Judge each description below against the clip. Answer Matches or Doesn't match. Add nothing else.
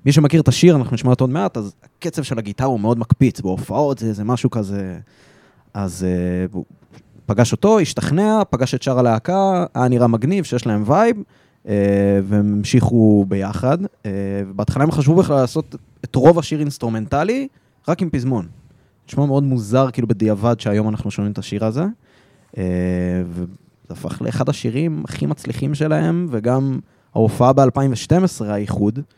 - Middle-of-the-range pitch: Doesn't match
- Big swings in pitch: Matches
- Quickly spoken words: Matches